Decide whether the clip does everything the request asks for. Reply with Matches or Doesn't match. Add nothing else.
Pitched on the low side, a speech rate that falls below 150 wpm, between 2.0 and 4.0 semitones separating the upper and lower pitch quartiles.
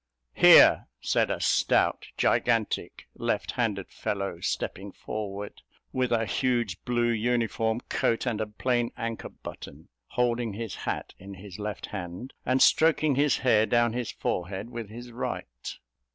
Matches